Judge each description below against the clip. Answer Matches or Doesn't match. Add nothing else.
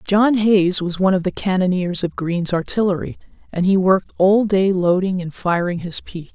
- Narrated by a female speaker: Matches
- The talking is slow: Doesn't match